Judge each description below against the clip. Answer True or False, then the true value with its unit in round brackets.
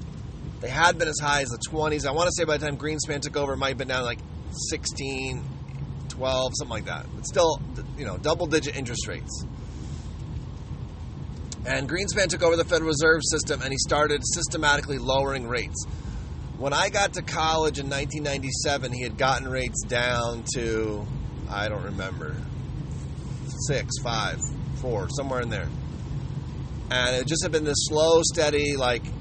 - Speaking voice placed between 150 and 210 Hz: False (135 Hz)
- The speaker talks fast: False (165 wpm)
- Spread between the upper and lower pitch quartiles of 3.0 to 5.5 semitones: True (3.3 semitones)